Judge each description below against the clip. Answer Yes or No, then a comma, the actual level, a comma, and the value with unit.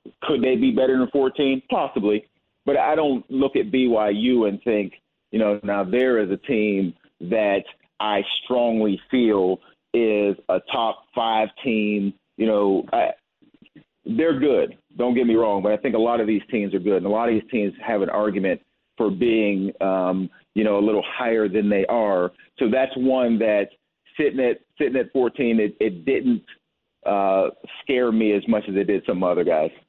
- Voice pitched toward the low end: Yes, low, 110 Hz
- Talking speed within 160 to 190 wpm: Yes, average, 185 wpm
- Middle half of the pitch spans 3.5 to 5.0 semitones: Yes, average, 3.8 semitones